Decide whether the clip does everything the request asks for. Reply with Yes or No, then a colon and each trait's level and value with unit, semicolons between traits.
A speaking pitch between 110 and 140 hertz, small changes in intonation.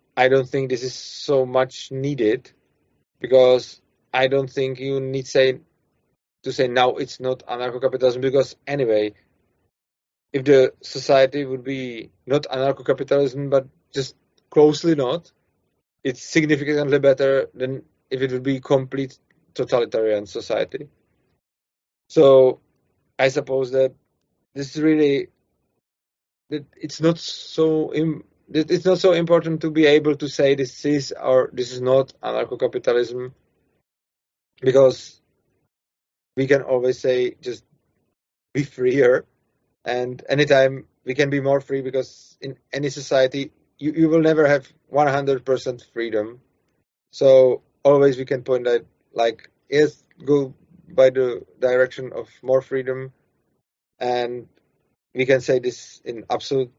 Yes: low, 135 Hz; narrow, 2.1 semitones